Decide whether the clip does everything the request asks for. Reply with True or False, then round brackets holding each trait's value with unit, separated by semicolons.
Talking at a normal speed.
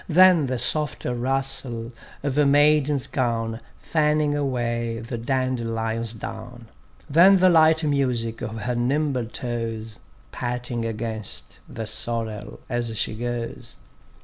False (120 wpm)